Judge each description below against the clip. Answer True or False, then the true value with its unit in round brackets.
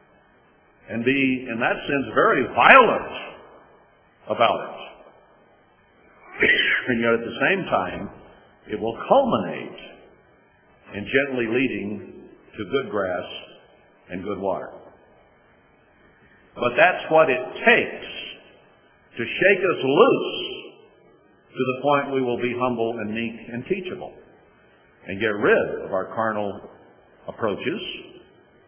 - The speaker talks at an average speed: False (115 wpm)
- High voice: False (135 Hz)